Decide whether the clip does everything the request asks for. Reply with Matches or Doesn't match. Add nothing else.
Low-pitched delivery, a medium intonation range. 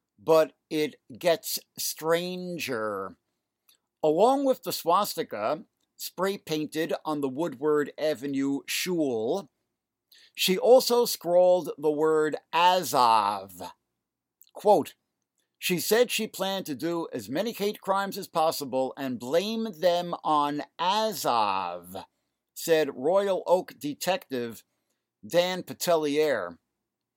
Doesn't match